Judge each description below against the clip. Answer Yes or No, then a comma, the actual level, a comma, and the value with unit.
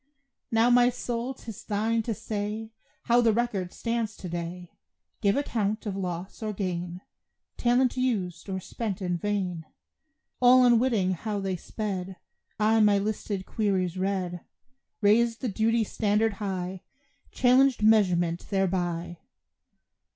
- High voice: Yes, high, 205 Hz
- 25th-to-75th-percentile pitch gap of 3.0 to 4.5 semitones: Yes, average, 3.7 semitones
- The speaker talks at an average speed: No, slow, 130 wpm